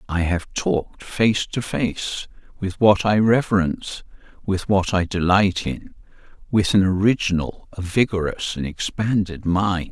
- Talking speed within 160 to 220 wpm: No, slow, 135 wpm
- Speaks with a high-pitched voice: No, very low, 95 Hz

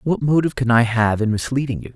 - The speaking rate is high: Yes, fast, 245 wpm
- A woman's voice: No, male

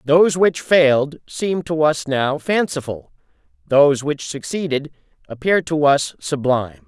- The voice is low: No, medium, 150 Hz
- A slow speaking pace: Yes, slow, 130 wpm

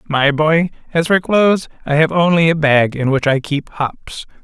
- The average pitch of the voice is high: No, medium, 155 Hz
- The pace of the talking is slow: No, fast, 205 wpm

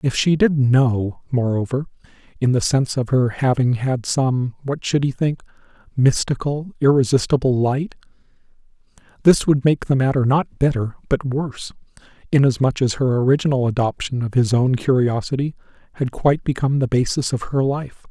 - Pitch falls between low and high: No, low, 130 Hz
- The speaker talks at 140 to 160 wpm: Yes, average, 145 wpm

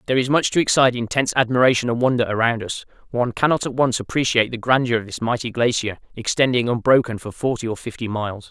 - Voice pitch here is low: Yes, low, 120 Hz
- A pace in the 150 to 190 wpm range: No, fast, 205 wpm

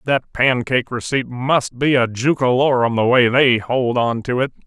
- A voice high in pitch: No, low, 125 Hz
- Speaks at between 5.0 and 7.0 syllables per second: No, 4.6 syllables/s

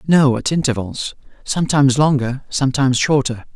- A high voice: No, low, 135 Hz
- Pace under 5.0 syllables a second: No, 5.6 syllables/s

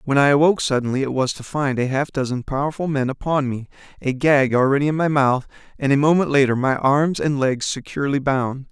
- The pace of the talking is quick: Yes, fast, 215 wpm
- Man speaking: Yes, male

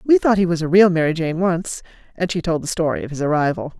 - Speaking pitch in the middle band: Yes, medium, 170 Hz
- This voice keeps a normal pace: No, fast, 270 wpm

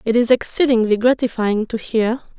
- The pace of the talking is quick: No, average, 150 wpm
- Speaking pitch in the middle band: No, high, 230 Hz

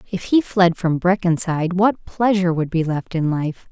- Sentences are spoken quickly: No, average, 195 wpm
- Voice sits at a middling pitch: Yes, medium, 180 Hz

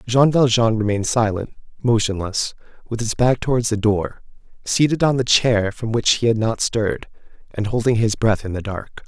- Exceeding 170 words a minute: Yes, average, 185 wpm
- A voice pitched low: Yes, low, 110 Hz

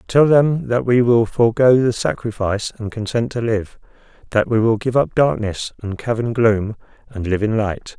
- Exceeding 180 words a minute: Yes, average, 190 wpm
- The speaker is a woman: No, male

